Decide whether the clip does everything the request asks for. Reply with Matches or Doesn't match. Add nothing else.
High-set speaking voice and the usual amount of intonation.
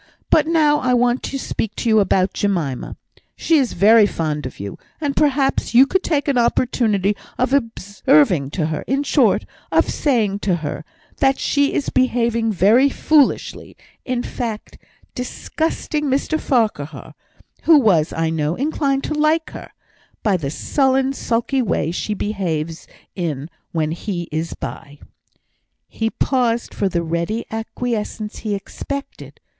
Doesn't match